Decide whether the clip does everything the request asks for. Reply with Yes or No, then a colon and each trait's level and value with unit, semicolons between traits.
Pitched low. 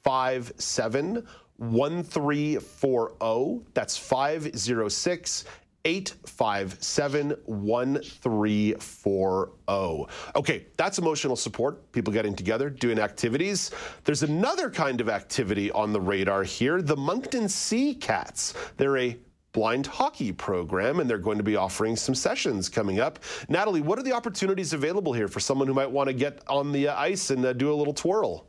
Yes: low, 130 Hz